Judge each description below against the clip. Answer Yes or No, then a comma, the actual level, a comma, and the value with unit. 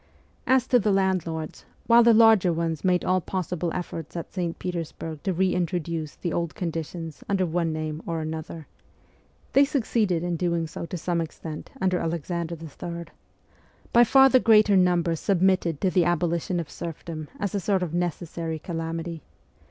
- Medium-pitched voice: Yes, medium, 170 Hz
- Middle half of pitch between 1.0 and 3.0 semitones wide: Yes, narrow, 2.4 semitones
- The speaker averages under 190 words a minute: Yes, average, 165 wpm